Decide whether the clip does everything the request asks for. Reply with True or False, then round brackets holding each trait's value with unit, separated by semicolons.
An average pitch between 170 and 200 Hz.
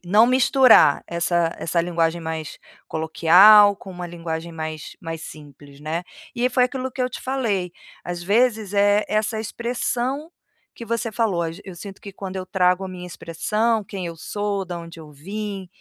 True (185 Hz)